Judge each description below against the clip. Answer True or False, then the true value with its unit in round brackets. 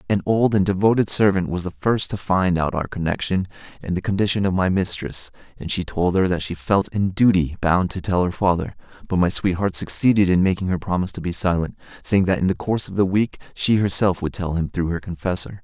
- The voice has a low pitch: True (90 Hz)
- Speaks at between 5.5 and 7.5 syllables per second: True (5.8 syllables/s)